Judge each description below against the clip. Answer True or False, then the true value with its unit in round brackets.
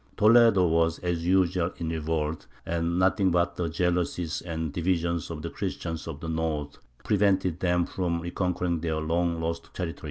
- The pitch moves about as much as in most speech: False (1.6 semitones)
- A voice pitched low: True (85 Hz)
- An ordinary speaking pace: True (160 wpm)